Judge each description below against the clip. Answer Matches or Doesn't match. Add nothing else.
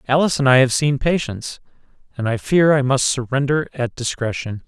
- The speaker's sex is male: Matches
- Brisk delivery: Doesn't match